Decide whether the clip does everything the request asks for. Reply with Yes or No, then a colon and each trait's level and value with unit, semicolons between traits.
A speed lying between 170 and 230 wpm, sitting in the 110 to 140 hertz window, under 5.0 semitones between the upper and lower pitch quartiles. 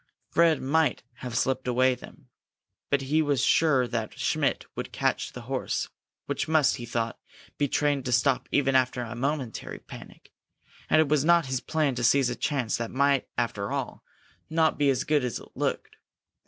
Yes: average, 180 wpm; low, 135 Hz; average, 3.1 semitones